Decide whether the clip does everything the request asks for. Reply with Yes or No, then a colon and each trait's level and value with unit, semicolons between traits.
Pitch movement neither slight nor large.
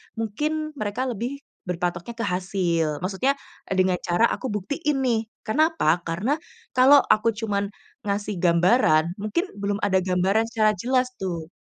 No: wide, 5.7 semitones